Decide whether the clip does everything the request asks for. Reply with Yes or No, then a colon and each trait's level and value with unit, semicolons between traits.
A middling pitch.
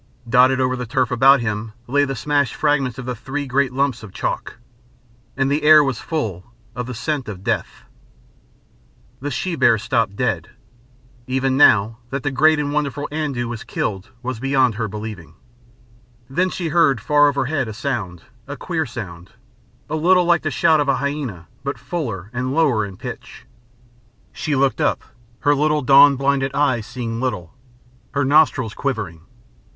No: low, 130 Hz